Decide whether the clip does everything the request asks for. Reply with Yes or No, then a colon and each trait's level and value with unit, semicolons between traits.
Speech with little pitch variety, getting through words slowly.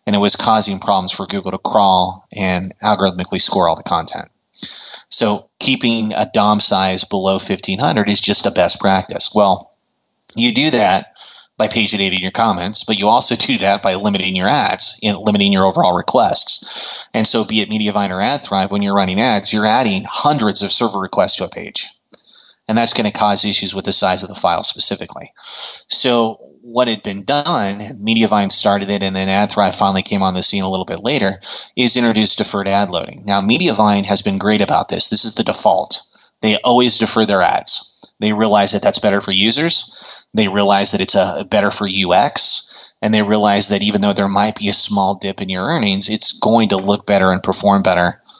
No: narrow, 1.9 semitones; average, 200 wpm